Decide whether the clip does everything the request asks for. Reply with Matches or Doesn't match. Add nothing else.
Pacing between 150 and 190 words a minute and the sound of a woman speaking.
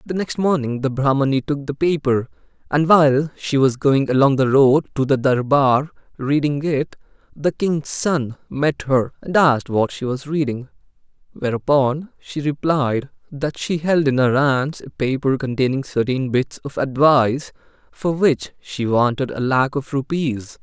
Doesn't match